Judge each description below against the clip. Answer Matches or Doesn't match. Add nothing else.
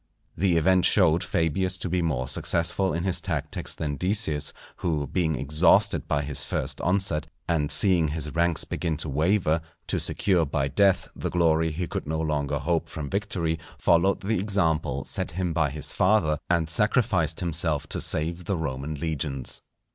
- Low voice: Matches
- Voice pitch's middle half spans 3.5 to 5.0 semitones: Doesn't match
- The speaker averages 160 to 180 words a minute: Matches